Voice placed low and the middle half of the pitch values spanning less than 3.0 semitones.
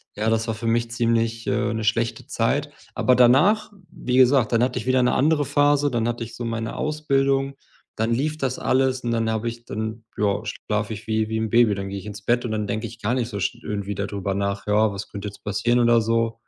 Yes: low, 115 Hz; narrow, 2.6 semitones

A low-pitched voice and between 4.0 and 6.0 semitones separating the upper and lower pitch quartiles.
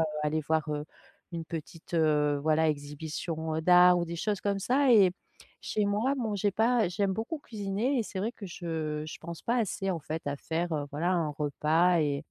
No: medium, 170 Hz; average, 4.6 semitones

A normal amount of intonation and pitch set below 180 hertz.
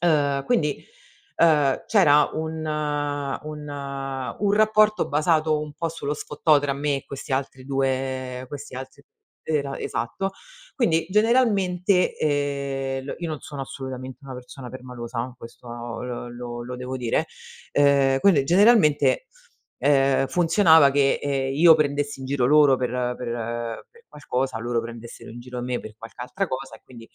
Yes: average, 3.4 semitones; medium, 140 Hz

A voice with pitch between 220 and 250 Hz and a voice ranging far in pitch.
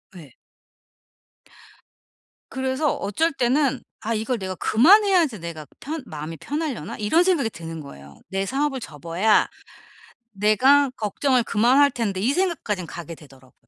Yes: high, 225 Hz; wide, 8.5 semitones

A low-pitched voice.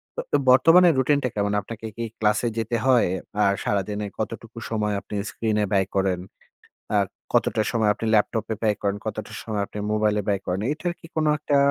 Yes: low, 110 Hz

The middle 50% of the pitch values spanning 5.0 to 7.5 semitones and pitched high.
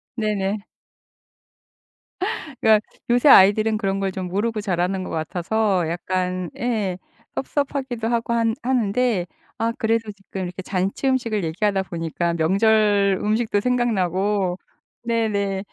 No: average, 3.4 semitones; high, 205 Hz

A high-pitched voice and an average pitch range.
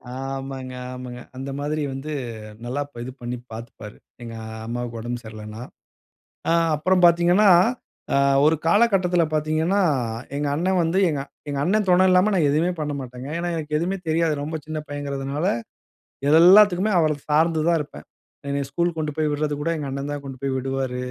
No: medium, 150 Hz; average, 4.1 semitones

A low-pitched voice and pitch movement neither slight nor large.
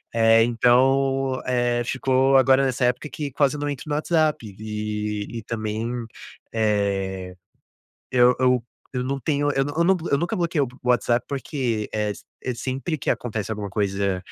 Yes: low, 125 Hz; average, 4.0 semitones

